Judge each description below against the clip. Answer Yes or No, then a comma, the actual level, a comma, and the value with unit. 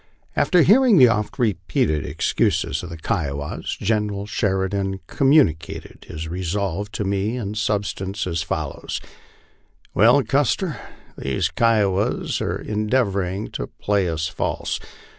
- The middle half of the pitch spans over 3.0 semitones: Yes, average, 3.8 semitones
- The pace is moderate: No, slow, 120 wpm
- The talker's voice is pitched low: Yes, low, 100 Hz